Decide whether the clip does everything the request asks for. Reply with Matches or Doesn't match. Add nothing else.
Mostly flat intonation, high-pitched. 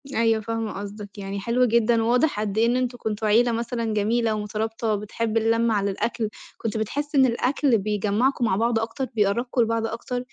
Matches